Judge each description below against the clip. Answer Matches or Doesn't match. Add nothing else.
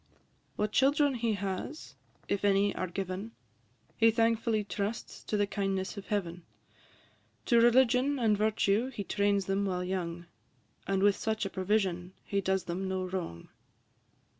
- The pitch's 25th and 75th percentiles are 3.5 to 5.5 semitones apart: Doesn't match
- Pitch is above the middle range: Matches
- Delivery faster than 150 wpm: Doesn't match